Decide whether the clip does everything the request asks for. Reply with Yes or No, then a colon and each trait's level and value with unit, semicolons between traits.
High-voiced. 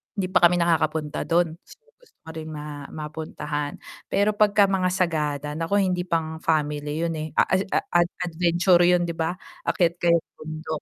No: medium, 165 Hz